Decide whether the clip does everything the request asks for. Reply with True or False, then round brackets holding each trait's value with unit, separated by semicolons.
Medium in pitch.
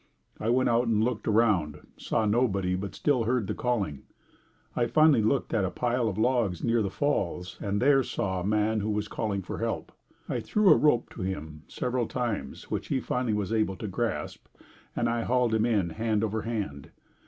False (110 Hz)